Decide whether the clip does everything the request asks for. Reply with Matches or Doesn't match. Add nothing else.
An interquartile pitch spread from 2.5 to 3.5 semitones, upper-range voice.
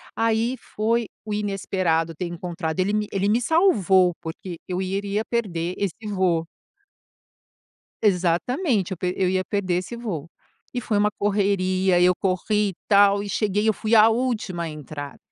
Matches